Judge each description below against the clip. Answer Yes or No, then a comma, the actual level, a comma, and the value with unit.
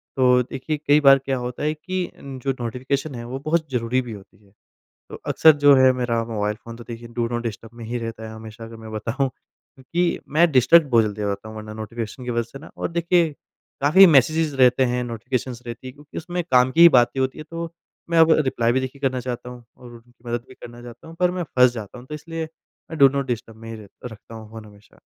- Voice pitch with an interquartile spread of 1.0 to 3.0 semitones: No, average, 3.5 semitones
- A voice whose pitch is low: Yes, low, 125 Hz